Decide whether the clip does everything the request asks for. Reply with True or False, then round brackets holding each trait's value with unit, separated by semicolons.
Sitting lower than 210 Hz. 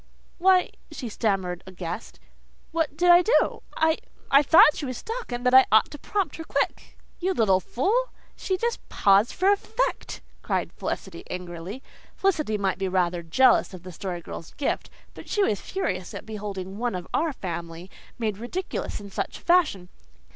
False (225 Hz)